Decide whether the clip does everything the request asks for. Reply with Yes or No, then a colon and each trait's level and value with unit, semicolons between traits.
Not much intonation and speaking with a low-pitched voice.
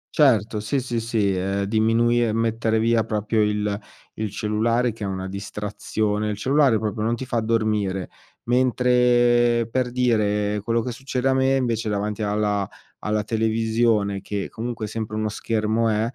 Yes: narrow, 2.2 semitones; low, 110 Hz